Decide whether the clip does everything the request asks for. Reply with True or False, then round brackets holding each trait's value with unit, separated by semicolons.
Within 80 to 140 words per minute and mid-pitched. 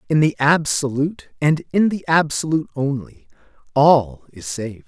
True (135 wpm; 145 Hz)